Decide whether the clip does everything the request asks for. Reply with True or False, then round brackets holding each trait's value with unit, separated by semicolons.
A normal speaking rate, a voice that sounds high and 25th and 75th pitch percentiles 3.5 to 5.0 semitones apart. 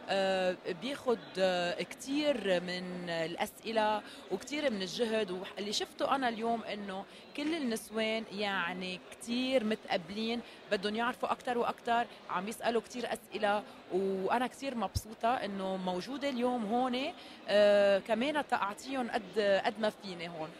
True (115 wpm; 220 Hz; 4.3 semitones)